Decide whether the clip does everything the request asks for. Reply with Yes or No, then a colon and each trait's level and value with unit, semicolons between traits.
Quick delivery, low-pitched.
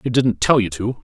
Yes: fast, 270 wpm; low, 110 Hz